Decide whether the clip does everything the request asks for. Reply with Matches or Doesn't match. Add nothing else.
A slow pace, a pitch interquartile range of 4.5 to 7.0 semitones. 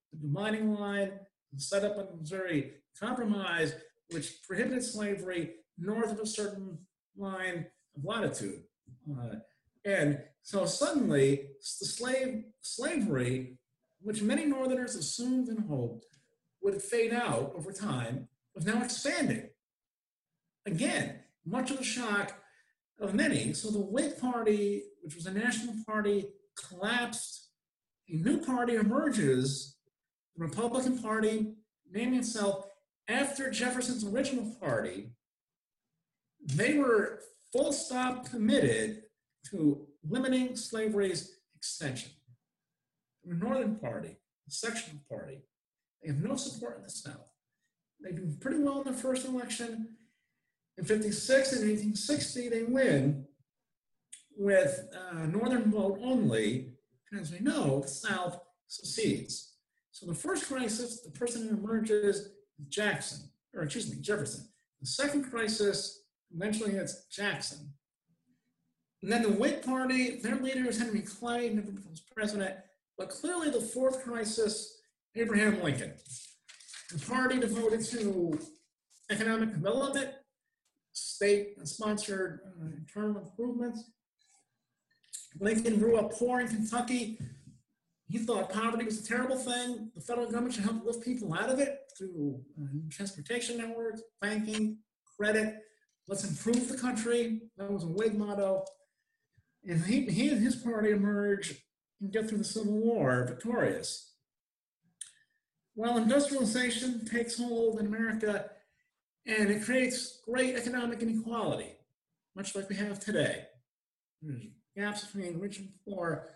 Matches